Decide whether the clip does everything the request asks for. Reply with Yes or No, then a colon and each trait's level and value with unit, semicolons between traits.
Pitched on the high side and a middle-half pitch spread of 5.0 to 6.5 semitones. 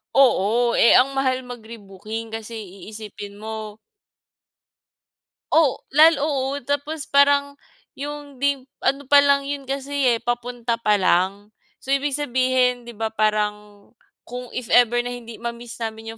No: high, 245 Hz; average, 4.0 semitones